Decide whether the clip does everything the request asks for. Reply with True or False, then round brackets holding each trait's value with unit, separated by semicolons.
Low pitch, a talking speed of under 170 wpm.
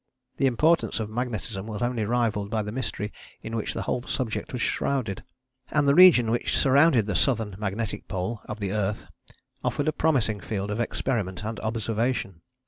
False (110 Hz; 175 wpm)